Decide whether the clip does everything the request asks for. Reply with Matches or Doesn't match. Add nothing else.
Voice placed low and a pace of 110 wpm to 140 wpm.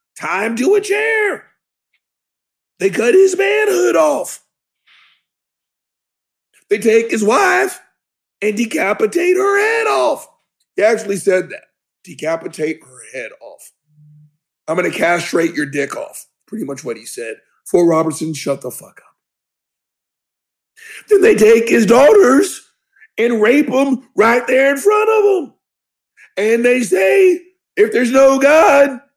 Doesn't match